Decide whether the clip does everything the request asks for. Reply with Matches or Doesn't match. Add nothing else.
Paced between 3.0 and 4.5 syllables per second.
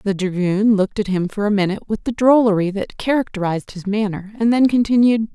Doesn't match